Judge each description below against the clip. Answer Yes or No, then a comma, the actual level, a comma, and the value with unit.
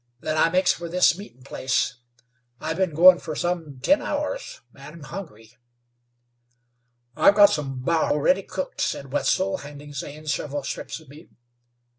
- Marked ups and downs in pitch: No, average, 4.6 semitones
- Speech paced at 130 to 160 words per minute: Yes, average, 155 wpm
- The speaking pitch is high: No, medium, 160 Hz